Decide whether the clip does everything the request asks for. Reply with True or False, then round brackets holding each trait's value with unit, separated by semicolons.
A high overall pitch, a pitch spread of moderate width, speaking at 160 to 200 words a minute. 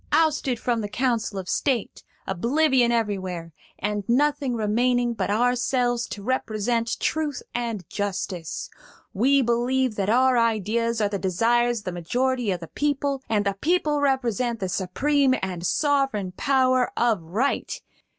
False (235 Hz; 4.2 semitones; 140 wpm)